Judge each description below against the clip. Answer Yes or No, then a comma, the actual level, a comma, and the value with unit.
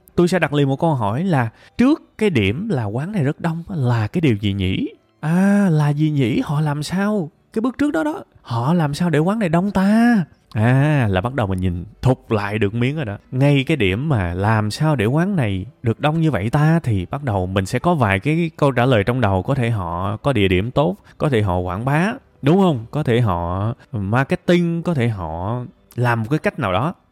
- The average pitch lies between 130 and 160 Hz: Yes, medium, 140 Hz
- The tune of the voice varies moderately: No, wide, 7.2 semitones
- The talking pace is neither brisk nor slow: Yes, average, 235 wpm